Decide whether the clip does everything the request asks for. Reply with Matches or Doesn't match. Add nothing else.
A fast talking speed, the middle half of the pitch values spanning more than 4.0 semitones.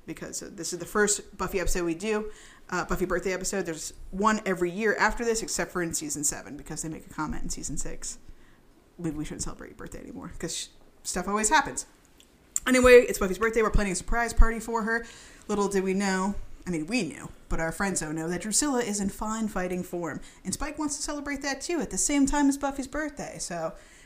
Matches